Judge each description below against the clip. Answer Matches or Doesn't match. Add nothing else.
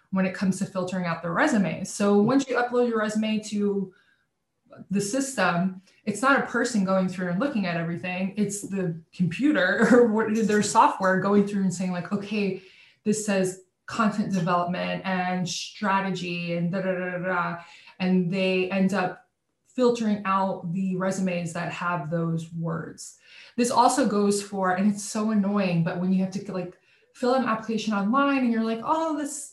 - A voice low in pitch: Doesn't match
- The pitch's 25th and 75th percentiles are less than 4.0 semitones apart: Matches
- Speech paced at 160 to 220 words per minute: Matches